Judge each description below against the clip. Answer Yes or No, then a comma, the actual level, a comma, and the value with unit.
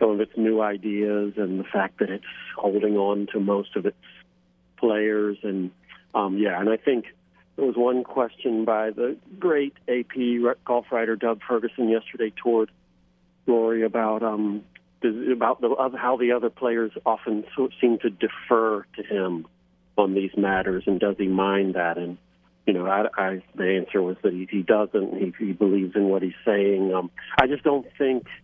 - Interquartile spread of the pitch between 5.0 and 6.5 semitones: No, average, 3.3 semitones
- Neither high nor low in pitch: No, low, 105 Hz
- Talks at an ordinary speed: Yes, average, 180 wpm